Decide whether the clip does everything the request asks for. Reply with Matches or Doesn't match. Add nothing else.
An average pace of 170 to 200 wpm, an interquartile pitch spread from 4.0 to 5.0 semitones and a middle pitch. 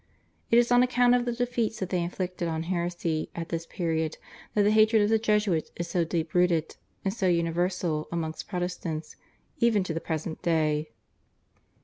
Matches